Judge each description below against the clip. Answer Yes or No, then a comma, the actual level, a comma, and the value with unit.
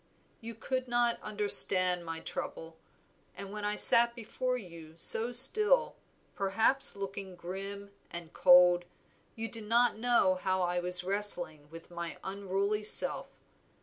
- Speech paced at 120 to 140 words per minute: Yes, slow, 135 wpm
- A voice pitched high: Yes, high, 200 Hz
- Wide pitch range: No, average, 4.2 semitones